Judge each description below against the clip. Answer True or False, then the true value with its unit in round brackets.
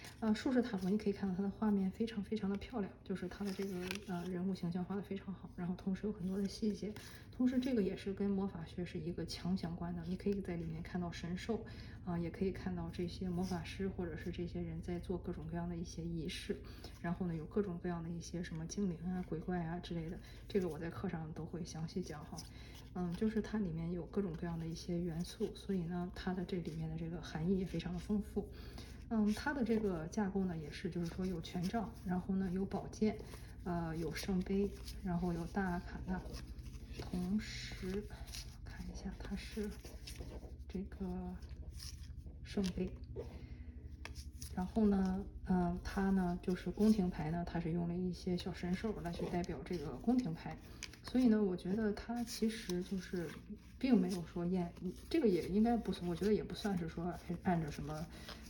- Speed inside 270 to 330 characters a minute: True (290 characters per minute)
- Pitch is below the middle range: False (180 Hz)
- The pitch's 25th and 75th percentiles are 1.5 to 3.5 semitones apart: True (2.6 semitones)